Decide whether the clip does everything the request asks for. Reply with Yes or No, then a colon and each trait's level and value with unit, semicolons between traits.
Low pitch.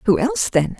No: high, 230 Hz